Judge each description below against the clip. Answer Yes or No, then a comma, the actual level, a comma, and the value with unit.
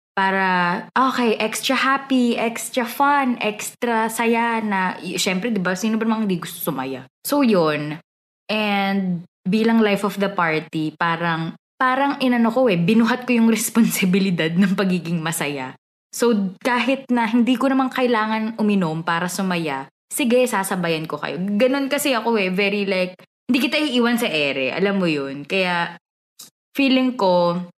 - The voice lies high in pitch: Yes, high, 205 Hz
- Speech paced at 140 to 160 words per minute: Yes, average, 150 wpm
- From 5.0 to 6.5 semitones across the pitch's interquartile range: Yes, average, 5.3 semitones